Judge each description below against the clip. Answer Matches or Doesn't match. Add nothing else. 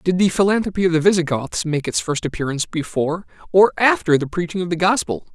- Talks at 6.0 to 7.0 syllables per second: Matches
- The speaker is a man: Matches